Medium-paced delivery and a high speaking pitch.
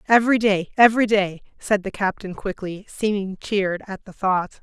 Yes: average, 170 wpm; high, 200 Hz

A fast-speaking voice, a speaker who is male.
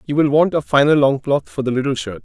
Yes: fast, 270 wpm; male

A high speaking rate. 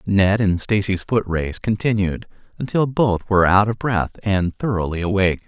No: average, 165 wpm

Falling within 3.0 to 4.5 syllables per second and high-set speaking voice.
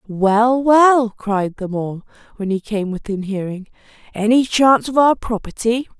Yes: 4.2 syllables/s; high, 220 Hz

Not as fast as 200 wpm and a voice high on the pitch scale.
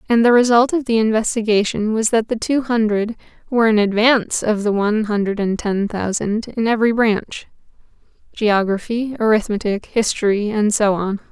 Yes: average, 155 wpm; high, 220 Hz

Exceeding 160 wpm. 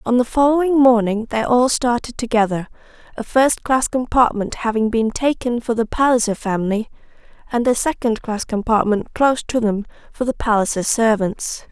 No: average, 155 wpm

